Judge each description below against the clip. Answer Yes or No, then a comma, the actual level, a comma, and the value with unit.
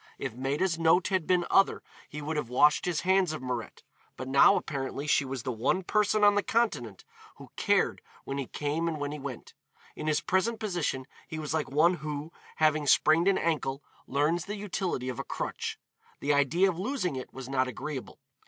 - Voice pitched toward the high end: No, medium, 155 Hz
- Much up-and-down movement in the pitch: No, average, 4.8 semitones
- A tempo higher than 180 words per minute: Yes, average, 200 wpm